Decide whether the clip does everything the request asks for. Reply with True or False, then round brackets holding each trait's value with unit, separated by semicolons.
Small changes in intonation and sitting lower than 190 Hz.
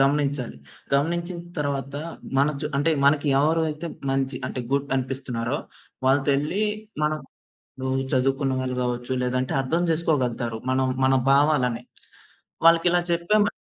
False (3.0 semitones; 140 Hz)